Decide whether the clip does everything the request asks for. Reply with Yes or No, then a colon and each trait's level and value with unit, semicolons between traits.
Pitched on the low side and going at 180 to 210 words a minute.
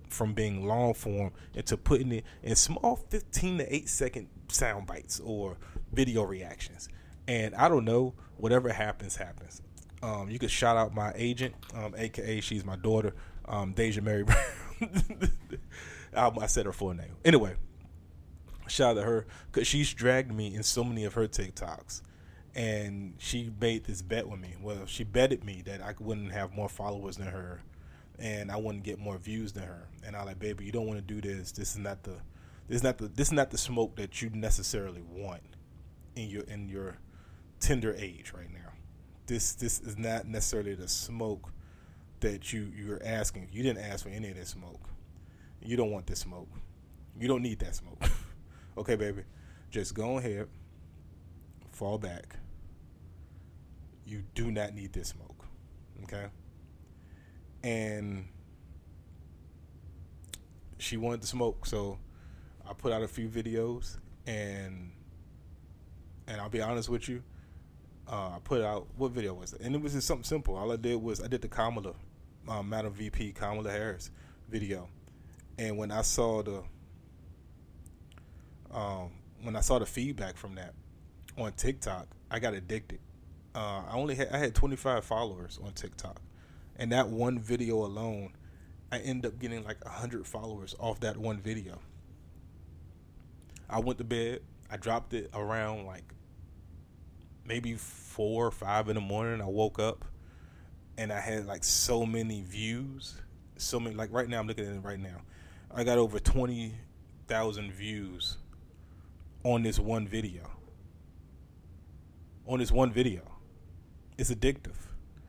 No: low, 100 Hz; average, 160 wpm